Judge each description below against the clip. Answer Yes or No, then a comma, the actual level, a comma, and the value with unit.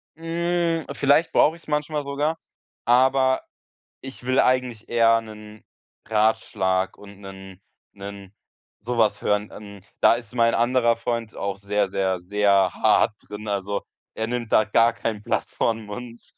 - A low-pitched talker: Yes, low, 115 Hz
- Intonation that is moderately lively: Yes, average, 4.0 semitones